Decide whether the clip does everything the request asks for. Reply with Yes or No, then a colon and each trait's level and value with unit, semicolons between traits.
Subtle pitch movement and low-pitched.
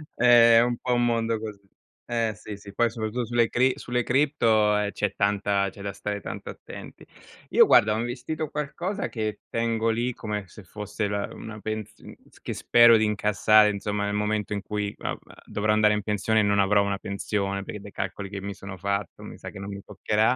Yes: narrow, 2.2 semitones; low, 105 Hz